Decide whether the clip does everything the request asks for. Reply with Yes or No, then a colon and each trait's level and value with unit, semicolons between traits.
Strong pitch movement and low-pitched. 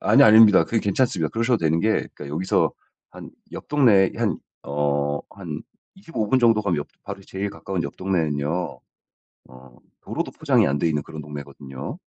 Yes: wide, 6.7 semitones; very low, 85 Hz